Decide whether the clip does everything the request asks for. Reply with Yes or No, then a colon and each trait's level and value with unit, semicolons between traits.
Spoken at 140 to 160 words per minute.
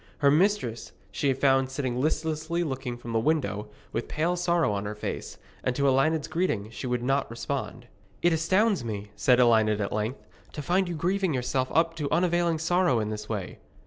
No: average, 185 wpm